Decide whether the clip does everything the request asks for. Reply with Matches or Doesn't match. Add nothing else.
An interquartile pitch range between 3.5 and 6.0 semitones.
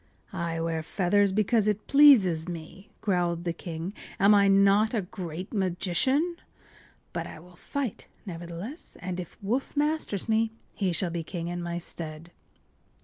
Matches